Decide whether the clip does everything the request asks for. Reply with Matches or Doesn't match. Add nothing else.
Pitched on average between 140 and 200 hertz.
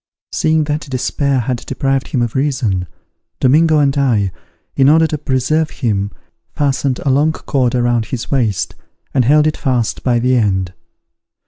Doesn't match